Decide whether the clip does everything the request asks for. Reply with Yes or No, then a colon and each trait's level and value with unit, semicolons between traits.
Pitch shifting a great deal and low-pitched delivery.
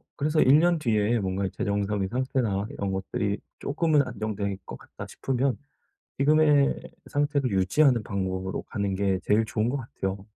Yes: wide, 6.0 semitones; low, 110 Hz